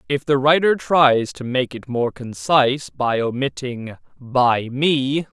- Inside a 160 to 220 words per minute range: No, average, 145 wpm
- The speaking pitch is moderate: No, low, 130 Hz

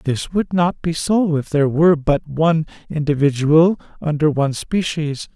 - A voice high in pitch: No, medium, 155 Hz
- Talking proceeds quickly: No, average, 170 wpm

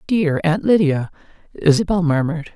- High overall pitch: No, medium, 180 Hz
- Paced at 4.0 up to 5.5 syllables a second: Yes, 5.2 syllables/s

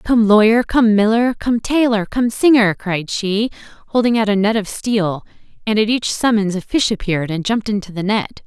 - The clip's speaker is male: No, female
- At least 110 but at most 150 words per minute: No, average, 200 wpm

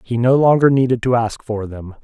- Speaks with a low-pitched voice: Yes, low, 120 Hz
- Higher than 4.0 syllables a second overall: Yes, 5.3 syllables/s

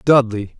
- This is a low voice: Yes, low, 120 Hz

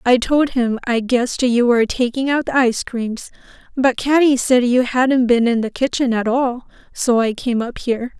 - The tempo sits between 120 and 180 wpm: No, fast, 205 wpm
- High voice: Yes, high, 245 Hz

